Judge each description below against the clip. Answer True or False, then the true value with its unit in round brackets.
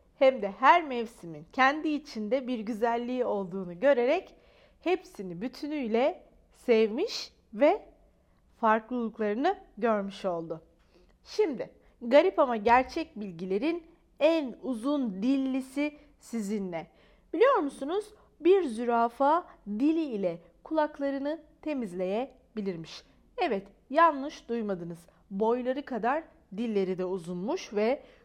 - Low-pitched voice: False (250 Hz)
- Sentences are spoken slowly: True (90 wpm)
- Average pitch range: False (6.2 semitones)